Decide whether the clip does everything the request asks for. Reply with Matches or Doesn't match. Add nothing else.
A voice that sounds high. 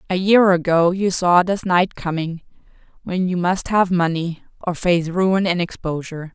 Doesn't match